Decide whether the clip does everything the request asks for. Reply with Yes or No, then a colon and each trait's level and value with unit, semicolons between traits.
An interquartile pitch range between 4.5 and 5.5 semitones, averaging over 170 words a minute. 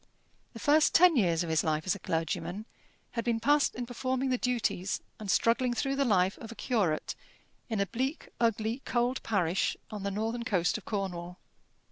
Yes: average, 4.9 semitones; average, 185 wpm